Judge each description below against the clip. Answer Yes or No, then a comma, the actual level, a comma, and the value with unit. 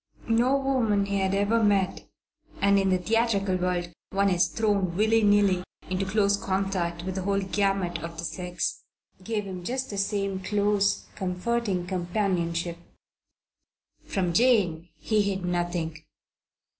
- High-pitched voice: Yes, high, 195 Hz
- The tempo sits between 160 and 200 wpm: No, average, 145 wpm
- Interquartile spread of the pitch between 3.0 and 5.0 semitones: No, narrow, 2.5 semitones